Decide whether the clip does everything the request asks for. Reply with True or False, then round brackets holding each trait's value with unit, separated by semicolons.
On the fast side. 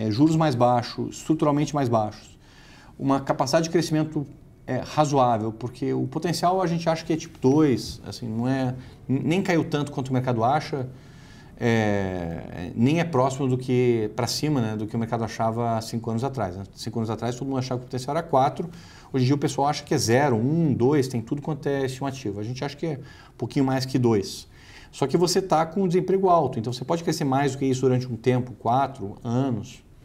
True (215 wpm)